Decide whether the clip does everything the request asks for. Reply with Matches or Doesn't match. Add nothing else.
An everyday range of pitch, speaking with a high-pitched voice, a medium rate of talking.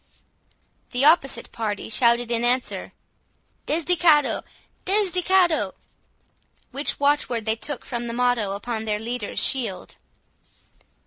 Doesn't match